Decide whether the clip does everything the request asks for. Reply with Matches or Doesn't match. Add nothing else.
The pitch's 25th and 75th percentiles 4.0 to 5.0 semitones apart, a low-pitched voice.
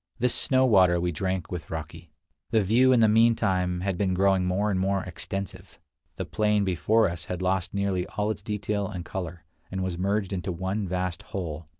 Doesn't match